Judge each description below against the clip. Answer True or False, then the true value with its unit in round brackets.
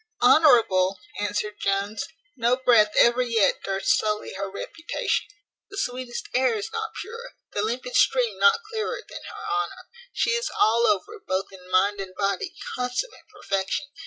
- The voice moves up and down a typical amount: False (8.7 semitones)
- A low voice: False (235 Hz)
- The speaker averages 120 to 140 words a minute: False (155 wpm)